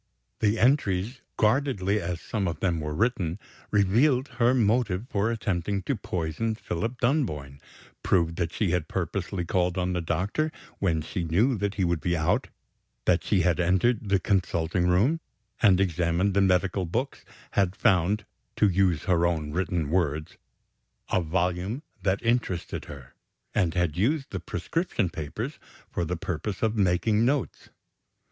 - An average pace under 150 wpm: No, average, 155 wpm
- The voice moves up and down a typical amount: Yes, average, 4.2 semitones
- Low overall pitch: Yes, very low, 95 Hz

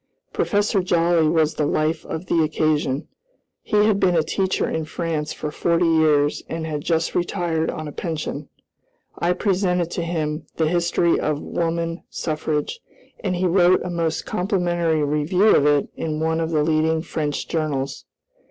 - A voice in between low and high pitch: Yes, medium, 165 Hz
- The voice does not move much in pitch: Yes, narrow, 2.2 semitones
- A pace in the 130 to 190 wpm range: Yes, average, 160 wpm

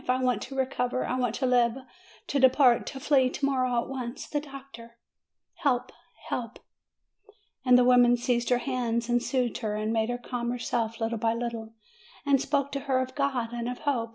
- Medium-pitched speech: No, very high, 250 Hz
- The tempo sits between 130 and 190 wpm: No, average, 200 wpm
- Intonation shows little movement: Yes, narrow, 2.1 semitones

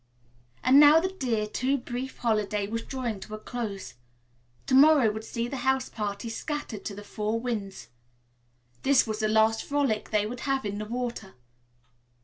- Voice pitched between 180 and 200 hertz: No, high, 230 Hz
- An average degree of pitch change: Yes, average, 3.7 semitones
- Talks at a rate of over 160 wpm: Yes, average, 170 wpm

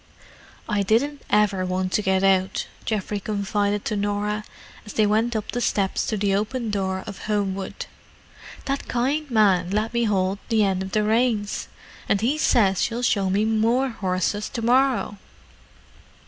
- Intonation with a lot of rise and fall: No, average, 2.7 semitones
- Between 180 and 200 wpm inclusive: No, average, 160 wpm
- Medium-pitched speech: No, high, 210 Hz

